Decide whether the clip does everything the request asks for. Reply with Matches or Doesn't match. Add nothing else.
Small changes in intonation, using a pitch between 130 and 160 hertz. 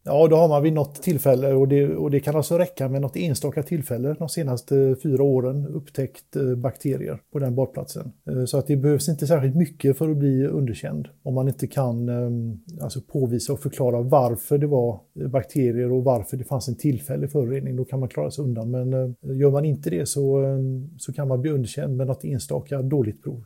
Matches